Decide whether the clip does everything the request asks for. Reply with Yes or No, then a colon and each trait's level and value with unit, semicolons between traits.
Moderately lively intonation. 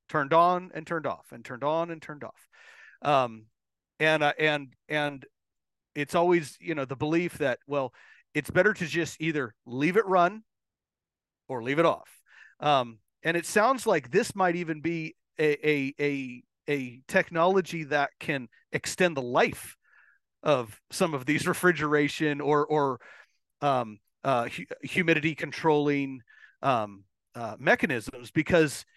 Yes: average, 3.8 semitones